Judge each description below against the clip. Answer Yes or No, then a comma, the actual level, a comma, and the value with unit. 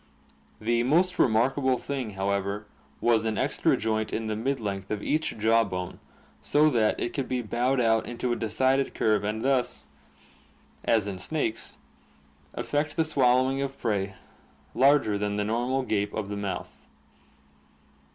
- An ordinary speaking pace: Yes, average, 150 wpm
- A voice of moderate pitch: No, low, 115 Hz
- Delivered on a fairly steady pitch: No, average, 4.0 semitones